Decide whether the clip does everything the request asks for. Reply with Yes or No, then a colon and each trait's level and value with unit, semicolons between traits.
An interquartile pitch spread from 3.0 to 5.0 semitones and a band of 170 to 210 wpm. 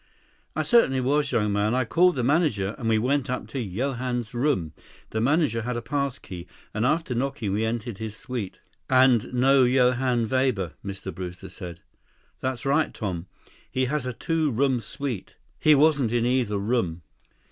Yes: average, 4.1 semitones; average, 175 wpm